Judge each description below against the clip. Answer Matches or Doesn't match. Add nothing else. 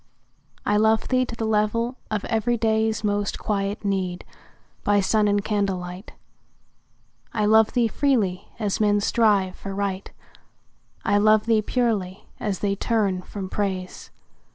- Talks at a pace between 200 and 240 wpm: Doesn't match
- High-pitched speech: Matches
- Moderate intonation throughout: Doesn't match